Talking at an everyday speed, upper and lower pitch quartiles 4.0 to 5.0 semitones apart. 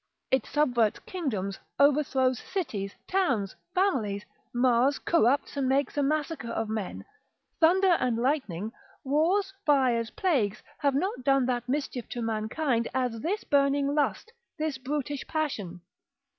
No: slow, 130 wpm; average, 4.6 semitones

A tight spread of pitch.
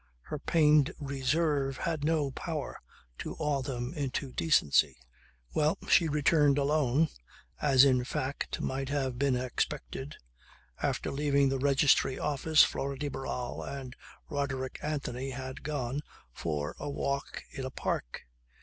Yes: narrow, 2.2 semitones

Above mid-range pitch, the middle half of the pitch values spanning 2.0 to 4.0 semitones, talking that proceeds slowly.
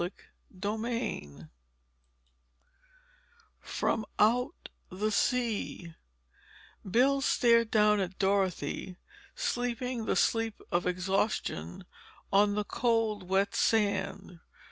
Yes: high, 210 Hz; average, 3.4 semitones; slow, 85 wpm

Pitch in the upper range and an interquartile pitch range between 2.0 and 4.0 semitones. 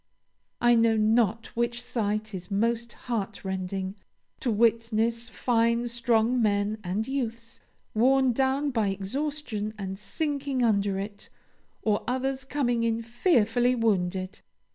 Yes: high, 230 Hz; average, 2.8 semitones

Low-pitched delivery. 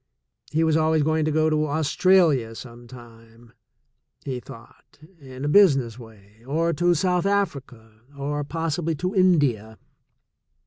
No: medium, 145 Hz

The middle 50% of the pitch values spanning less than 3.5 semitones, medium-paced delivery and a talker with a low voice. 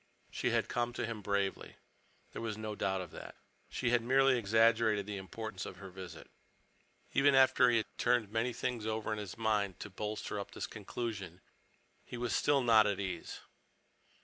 Yes: average, 3.1 semitones; average, 180 wpm; low, 110 Hz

